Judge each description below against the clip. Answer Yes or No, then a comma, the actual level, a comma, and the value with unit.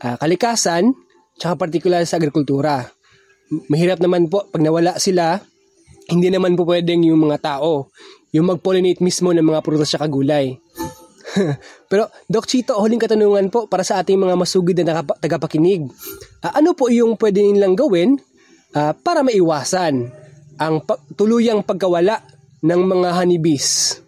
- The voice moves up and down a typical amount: Yes, average, 4.4 semitones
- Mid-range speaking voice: Yes, medium, 180 Hz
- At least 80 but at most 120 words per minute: No, average, 145 wpm